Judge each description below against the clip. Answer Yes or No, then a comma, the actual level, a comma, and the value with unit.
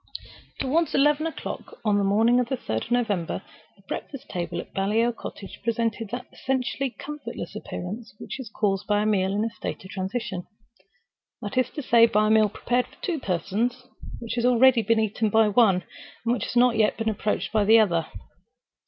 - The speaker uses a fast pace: No, average, 190 wpm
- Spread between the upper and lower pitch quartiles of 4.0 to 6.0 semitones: No, average, 3.4 semitones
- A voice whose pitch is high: Yes, high, 220 Hz